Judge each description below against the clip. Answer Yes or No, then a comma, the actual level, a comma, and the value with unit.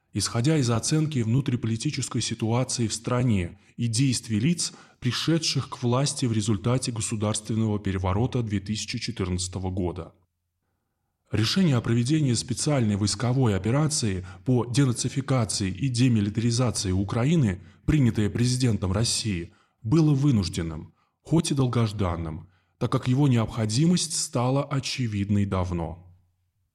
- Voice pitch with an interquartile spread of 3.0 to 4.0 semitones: No, average, 4.4 semitones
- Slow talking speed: Yes, slow, 100 wpm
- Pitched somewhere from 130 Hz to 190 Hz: No, low, 115 Hz